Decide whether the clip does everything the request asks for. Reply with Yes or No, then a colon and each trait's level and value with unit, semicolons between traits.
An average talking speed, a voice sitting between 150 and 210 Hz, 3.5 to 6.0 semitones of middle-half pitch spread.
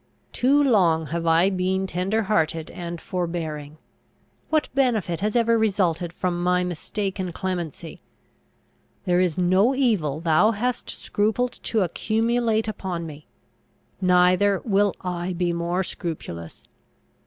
No: slow, 120 wpm; medium, 185 Hz; average, 4.0 semitones